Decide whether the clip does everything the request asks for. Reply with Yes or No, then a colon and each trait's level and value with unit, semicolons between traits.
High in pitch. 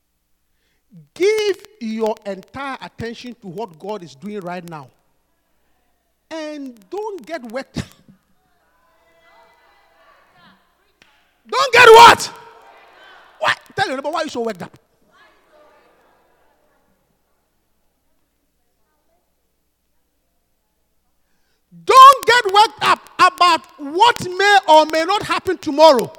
Yes: very high, 295 Hz